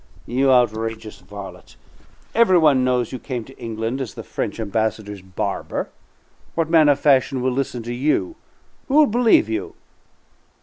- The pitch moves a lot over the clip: No, average, 4.5 semitones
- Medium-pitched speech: No, low, 125 Hz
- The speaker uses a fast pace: No, average, 150 wpm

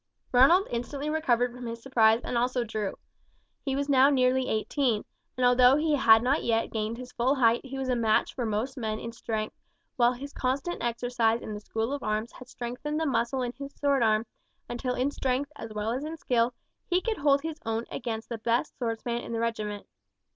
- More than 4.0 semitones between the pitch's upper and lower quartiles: No, average, 3.0 semitones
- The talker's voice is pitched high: Yes, high, 245 Hz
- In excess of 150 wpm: Yes, fast, 205 wpm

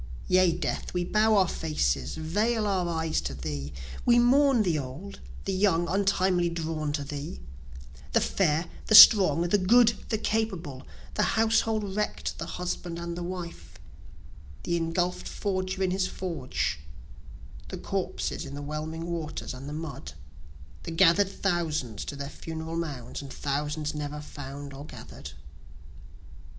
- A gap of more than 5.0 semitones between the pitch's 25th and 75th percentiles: No, average, 4.4 semitones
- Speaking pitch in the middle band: Yes, medium, 170 Hz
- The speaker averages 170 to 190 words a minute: No, average, 145 wpm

